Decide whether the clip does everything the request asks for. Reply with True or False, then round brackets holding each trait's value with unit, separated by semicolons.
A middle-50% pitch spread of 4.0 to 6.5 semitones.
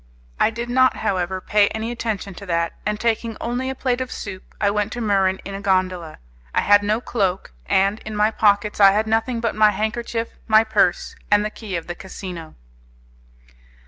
False (2.7 semitones)